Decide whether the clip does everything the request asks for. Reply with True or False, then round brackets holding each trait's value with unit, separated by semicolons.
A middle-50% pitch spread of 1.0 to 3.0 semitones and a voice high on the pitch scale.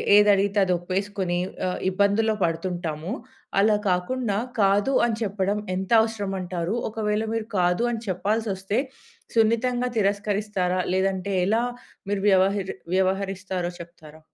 True (2.5 semitones; 195 Hz)